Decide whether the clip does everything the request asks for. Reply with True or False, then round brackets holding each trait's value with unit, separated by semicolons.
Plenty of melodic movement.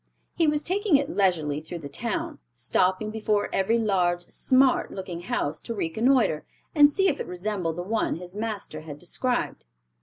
True (6.7 semitones)